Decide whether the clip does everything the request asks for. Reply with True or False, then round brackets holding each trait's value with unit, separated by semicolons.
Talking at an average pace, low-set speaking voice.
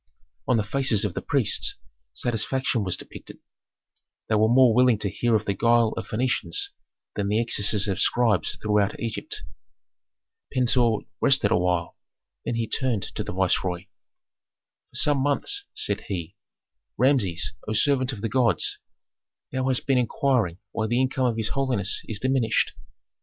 True (150 wpm; 115 Hz)